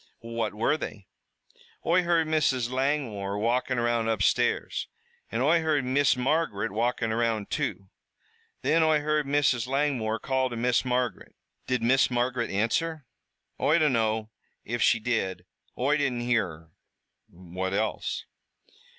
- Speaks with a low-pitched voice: Yes, low, 125 Hz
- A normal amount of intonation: Yes, average, 4.3 semitones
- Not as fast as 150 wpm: Yes, slow, 135 wpm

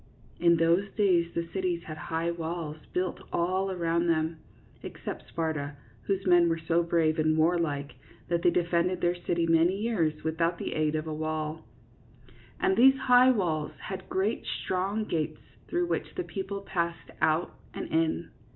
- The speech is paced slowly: No, average, 175 wpm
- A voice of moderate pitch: Yes, medium, 170 Hz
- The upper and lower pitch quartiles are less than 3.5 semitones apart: Yes, average, 2.7 semitones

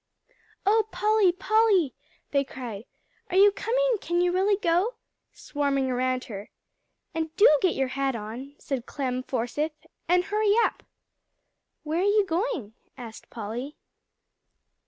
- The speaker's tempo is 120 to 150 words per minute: Yes, slow, 135 wpm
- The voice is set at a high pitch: Yes, very high, 320 Hz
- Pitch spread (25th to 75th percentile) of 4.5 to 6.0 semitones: No, wide, 7.9 semitones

